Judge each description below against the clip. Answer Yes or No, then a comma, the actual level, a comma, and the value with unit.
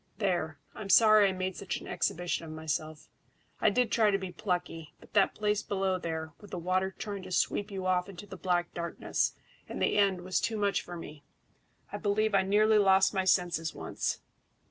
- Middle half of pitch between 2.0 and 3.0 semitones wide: Yes, narrow, 2.6 semitones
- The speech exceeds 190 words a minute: Yes, average, 200 wpm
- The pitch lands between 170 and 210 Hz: Yes, high, 190 Hz